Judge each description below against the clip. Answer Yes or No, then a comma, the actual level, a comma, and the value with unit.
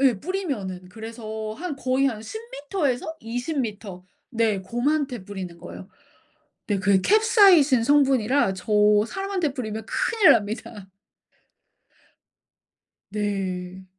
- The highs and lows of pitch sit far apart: Yes, wide, 6.2 semitones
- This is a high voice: Yes, high, 230 Hz